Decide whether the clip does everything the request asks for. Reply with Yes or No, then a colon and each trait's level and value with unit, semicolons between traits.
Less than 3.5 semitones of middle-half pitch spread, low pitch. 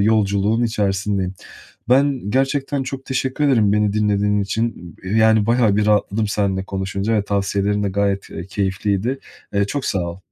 Yes: narrow, 2.6 semitones; low, 105 Hz